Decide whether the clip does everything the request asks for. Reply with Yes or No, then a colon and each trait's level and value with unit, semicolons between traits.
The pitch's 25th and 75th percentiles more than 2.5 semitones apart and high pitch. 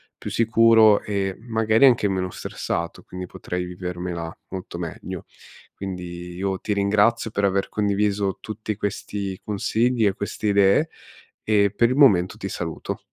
No: average, 2.9 semitones; low, 100 Hz